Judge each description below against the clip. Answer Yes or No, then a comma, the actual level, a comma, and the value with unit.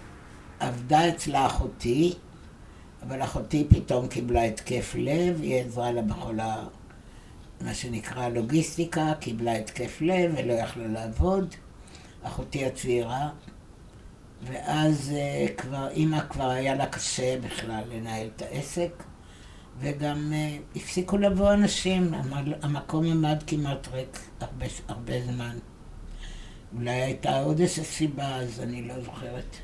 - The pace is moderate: Yes, average, 110 wpm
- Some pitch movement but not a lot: Yes, average, 4.6 semitones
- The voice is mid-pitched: No, low, 130 Hz